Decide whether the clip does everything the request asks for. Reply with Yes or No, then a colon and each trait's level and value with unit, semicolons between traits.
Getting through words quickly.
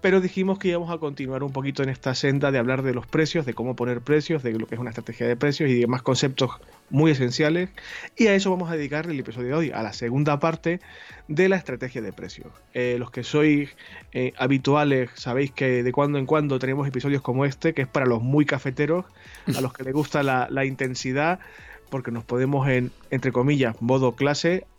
Yes: fast, 220 wpm